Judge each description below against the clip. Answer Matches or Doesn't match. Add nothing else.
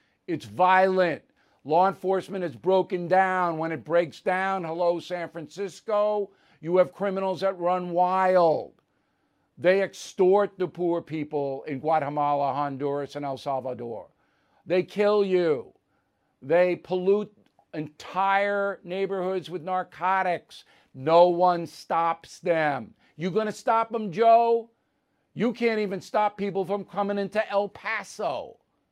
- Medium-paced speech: Doesn't match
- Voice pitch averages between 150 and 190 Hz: Matches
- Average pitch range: Matches